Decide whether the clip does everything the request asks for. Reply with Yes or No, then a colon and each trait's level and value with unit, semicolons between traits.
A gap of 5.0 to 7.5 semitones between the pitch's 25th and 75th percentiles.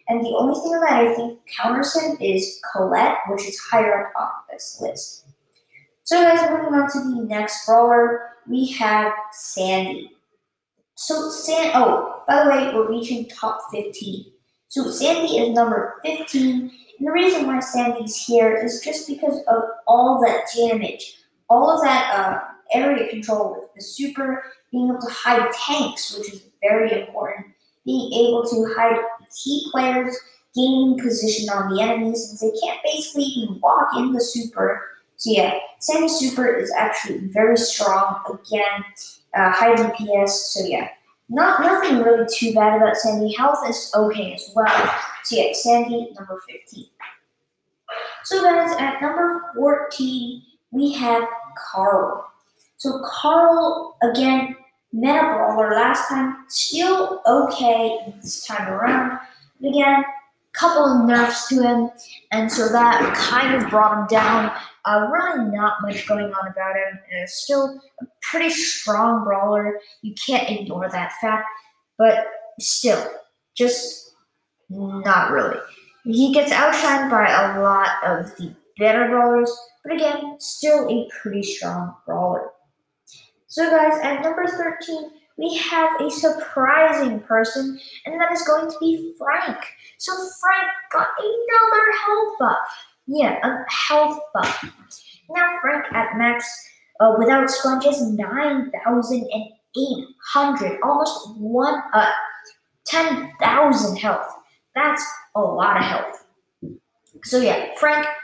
Yes: average, 5.3 semitones